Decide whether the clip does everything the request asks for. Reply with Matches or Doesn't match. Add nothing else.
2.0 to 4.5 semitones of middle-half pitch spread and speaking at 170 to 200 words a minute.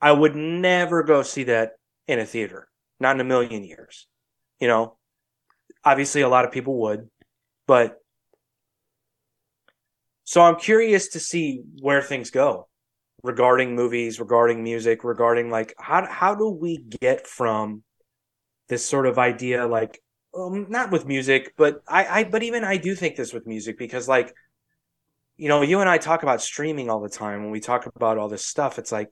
Doesn't match